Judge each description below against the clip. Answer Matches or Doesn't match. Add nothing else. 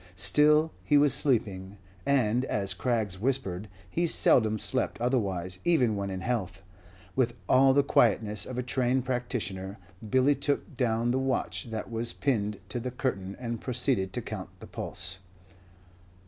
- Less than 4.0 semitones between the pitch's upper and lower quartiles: Doesn't match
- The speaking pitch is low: Matches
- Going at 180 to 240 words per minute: Doesn't match